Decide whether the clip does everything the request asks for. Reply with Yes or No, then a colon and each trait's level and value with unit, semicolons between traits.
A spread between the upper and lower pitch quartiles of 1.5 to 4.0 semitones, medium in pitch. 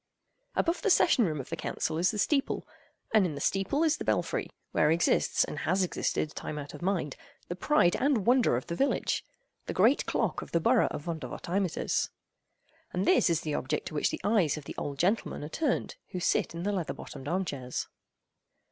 No: wide, 5.6 semitones; medium, 175 Hz